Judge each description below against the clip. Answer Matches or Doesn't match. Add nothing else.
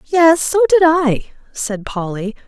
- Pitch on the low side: Doesn't match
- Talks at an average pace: Matches